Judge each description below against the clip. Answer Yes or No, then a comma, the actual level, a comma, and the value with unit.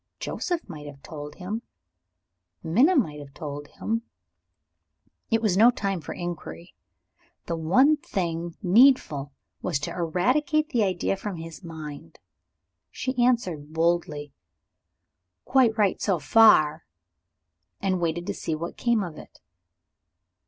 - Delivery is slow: Yes, slow, 125 wpm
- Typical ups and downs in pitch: No, wide, 6.1 semitones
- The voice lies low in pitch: No, medium, 175 Hz